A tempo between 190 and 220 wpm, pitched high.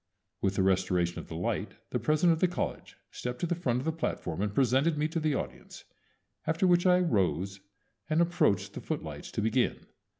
No: average, 200 wpm; low, 135 Hz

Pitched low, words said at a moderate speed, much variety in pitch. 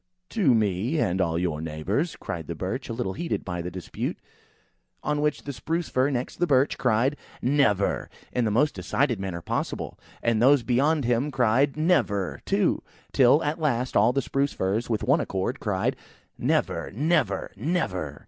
Yes: low, 120 Hz; average, 175 wpm; wide, 6.9 semitones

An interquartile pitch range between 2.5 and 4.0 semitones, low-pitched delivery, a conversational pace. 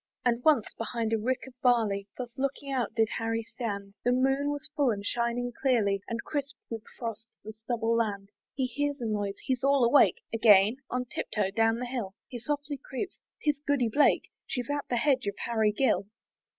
No: average, 3.4 semitones; high, 235 Hz; average, 195 wpm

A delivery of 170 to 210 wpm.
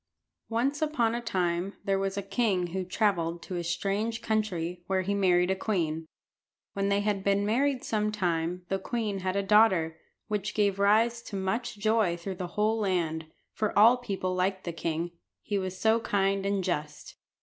Yes: average, 180 wpm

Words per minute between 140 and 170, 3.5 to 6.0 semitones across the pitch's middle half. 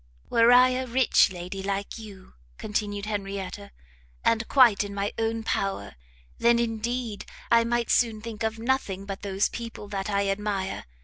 No: average, 160 wpm; average, 2.8 semitones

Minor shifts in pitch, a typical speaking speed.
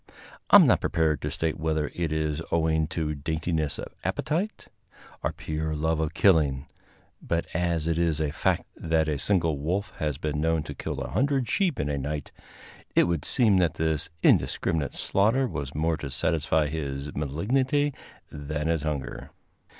Yes: narrow, 2.1 semitones; average, 170 wpm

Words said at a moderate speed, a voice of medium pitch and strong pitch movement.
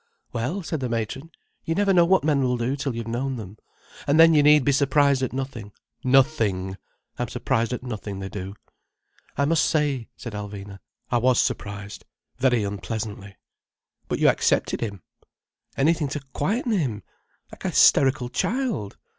No: average, 160 wpm; low, 125 Hz; wide, 5.7 semitones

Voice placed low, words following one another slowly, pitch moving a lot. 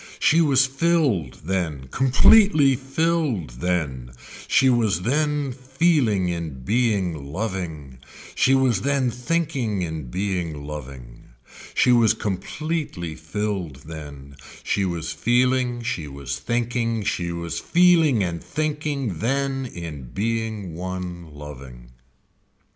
Yes: low, 100 Hz; slow, 110 wpm; wide, 8.6 semitones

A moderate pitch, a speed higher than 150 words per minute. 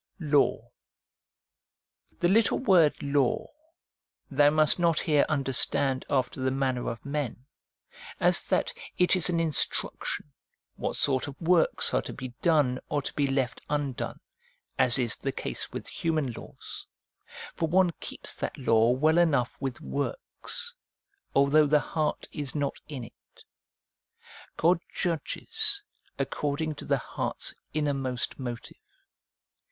No: medium, 145 Hz; slow, 135 wpm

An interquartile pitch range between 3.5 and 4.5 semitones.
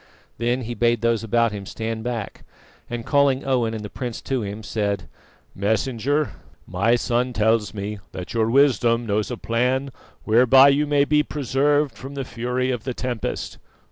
No: average, 3.1 semitones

